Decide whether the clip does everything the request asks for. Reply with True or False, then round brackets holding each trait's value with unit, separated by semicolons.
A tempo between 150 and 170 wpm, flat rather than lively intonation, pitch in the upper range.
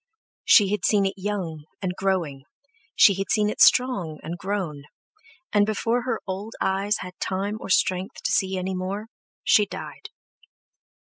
True (160 wpm; 2.1 semitones; 195 Hz)